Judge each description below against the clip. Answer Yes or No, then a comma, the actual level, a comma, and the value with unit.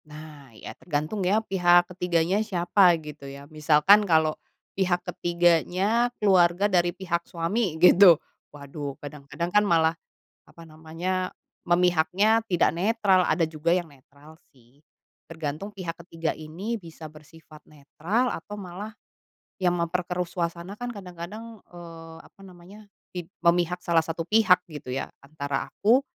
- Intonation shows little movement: No, average, 3.0 semitones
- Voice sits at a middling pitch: Yes, medium, 175 Hz